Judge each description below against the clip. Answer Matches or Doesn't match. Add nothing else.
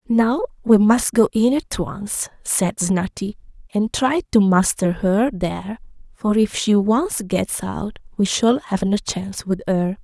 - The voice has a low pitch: Doesn't match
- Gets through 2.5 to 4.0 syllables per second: Matches